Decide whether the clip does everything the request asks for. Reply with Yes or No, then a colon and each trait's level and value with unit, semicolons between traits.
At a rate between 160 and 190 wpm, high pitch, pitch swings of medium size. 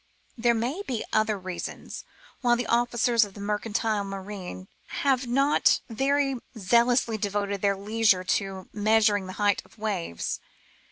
No: slow, 135 wpm; high, 215 Hz; average, 3.1 semitones